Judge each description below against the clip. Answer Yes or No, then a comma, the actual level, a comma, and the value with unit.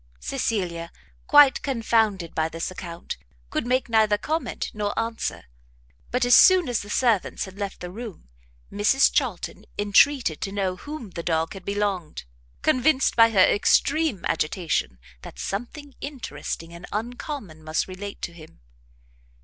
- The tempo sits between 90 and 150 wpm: Yes, average, 145 wpm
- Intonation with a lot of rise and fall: Yes, wide, 5.8 semitones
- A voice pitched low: No, high, 205 Hz